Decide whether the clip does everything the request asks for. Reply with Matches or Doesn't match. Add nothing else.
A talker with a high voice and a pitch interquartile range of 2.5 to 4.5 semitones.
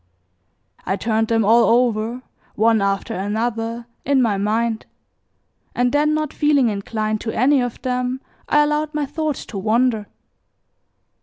Matches